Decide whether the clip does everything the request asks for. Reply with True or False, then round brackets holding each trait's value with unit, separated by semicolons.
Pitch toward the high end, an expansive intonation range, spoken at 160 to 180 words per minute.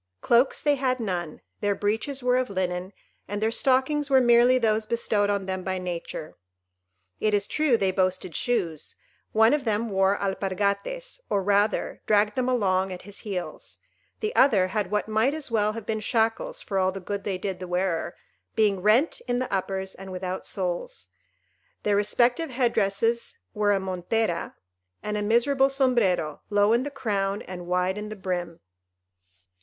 False (205 Hz; 3.9 semitones; 170 wpm)